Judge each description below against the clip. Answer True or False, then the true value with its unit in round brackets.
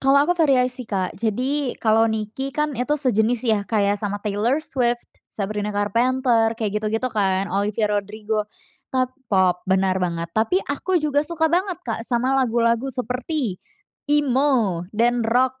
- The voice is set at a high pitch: True (230 Hz)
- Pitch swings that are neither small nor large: True (4.0 semitones)